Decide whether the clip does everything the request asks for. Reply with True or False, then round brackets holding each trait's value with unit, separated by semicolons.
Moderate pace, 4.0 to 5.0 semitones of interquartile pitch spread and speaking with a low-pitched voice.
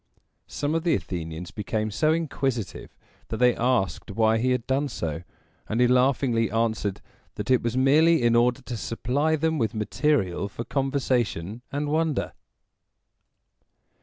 True (145 wpm; 4.3 semitones; 125 Hz)